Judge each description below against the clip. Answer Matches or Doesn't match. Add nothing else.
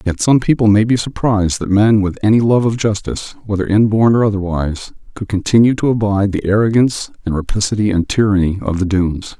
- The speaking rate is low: Doesn't match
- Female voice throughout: Doesn't match